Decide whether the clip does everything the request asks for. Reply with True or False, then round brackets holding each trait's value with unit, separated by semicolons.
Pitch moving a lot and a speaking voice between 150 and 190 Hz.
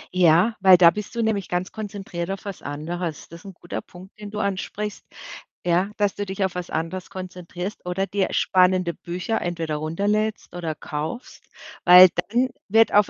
False (2.8 semitones; 185 Hz)